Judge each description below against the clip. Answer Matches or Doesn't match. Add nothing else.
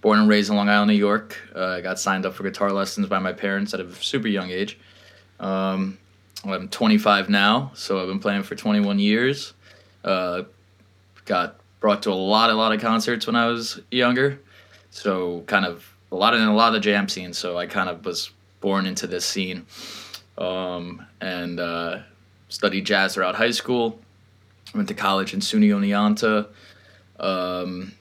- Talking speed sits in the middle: Matches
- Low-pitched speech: Matches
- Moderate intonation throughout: Doesn't match